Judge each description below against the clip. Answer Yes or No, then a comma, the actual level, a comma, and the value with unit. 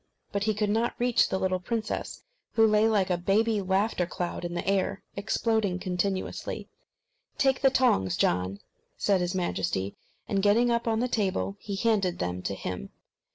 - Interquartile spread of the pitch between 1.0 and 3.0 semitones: No, average, 3.8 semitones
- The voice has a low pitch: No, high, 195 Hz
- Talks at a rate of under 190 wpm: Yes, average, 170 wpm